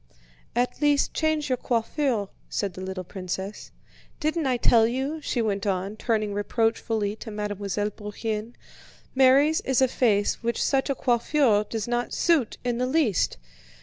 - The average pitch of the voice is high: Yes, high, 230 Hz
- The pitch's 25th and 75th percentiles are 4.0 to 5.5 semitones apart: Yes, average, 4.3 semitones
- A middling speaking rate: Yes, average, 150 wpm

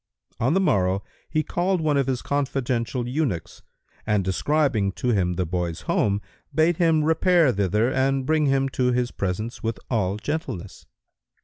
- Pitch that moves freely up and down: Yes, wide, 7.0 semitones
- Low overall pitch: Yes, low, 125 Hz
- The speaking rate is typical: Yes, average, 155 wpm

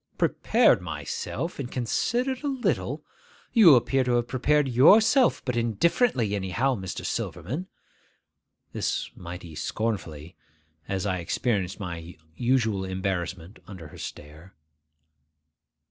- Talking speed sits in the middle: No, slow, 110 wpm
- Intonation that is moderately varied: No, wide, 6.8 semitones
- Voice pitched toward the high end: No, low, 110 Hz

